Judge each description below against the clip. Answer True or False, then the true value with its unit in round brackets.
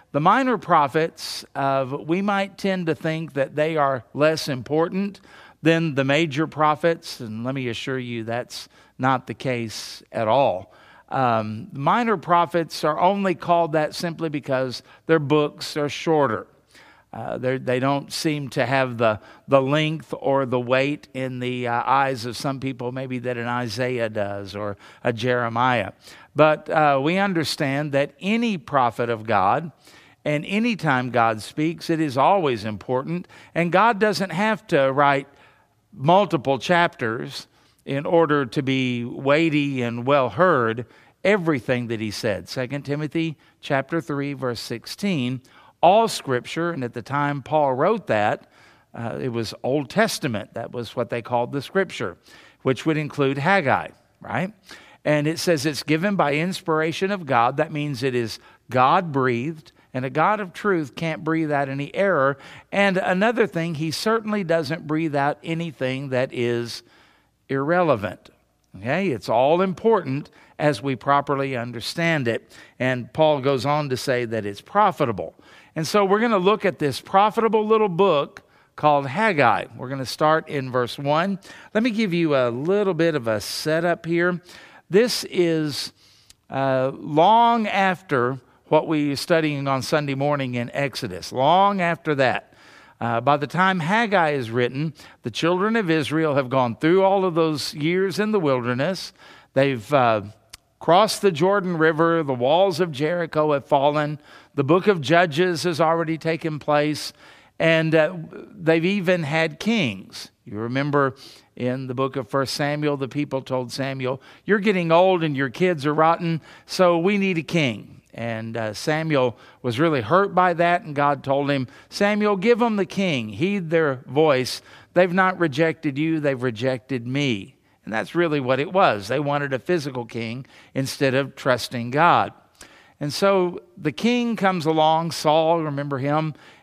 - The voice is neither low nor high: True (150 Hz)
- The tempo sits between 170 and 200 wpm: False (160 wpm)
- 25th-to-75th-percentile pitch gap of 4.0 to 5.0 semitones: True (4.7 semitones)